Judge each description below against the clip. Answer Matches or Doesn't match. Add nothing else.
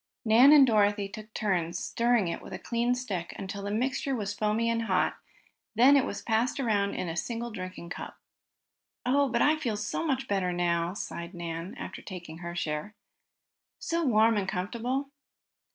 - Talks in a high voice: Matches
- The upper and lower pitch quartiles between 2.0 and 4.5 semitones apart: Doesn't match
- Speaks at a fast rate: Doesn't match